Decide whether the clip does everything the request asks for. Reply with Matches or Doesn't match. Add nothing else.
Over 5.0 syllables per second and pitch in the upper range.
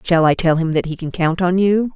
Doesn't match